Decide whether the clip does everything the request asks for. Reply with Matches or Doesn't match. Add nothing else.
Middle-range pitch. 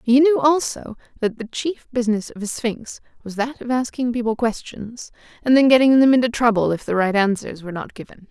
Doesn't match